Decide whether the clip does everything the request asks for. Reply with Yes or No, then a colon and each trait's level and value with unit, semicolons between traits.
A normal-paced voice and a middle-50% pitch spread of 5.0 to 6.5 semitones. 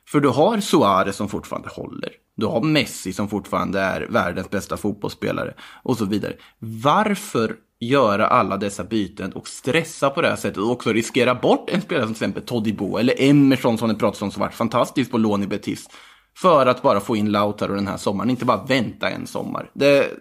No: fast, 200 wpm; wide, 5.4 semitones